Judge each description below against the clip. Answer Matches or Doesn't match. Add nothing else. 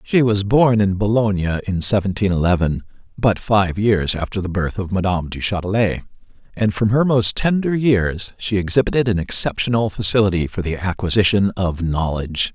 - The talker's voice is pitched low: Matches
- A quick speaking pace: Doesn't match